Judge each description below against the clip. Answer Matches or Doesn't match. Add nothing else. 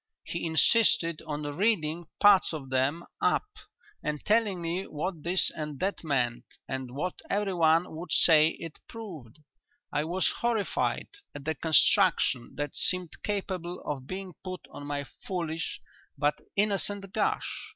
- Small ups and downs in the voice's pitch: Doesn't match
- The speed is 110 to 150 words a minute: Matches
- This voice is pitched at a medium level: Matches